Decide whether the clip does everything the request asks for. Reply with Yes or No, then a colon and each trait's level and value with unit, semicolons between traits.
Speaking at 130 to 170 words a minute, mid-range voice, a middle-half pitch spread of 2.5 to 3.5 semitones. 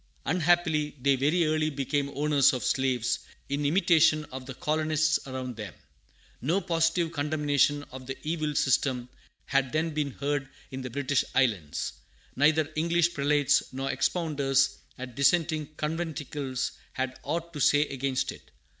Yes: average, 140 wpm; medium, 145 Hz; average, 2.8 semitones